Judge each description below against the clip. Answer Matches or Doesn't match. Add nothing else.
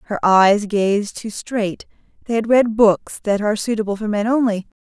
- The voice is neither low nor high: Doesn't match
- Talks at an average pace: Matches